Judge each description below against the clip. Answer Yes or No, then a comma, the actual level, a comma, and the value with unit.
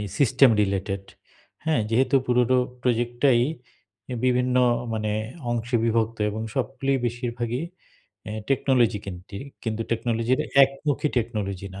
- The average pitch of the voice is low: Yes, low, 120 Hz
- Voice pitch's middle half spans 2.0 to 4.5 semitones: Yes, average, 2.7 semitones